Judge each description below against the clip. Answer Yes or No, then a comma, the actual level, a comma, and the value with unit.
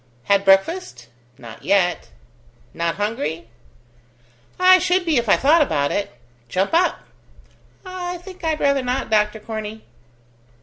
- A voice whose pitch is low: No, high, 220 Hz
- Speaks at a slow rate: Yes, slow, 130 wpm